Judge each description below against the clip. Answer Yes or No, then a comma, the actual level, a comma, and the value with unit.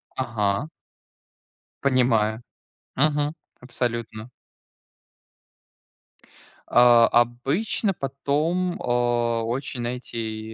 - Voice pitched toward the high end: No, low, 120 Hz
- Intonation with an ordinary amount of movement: Yes, average, 3.1 semitones